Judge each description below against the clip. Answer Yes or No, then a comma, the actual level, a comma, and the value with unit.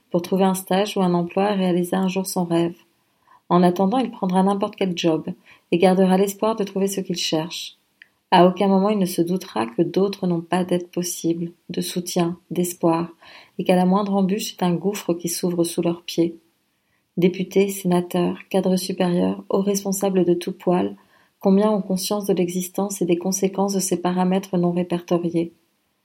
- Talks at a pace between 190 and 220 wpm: No, average, 180 wpm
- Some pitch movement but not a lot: No, narrow, 1.9 semitones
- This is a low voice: No, medium, 185 Hz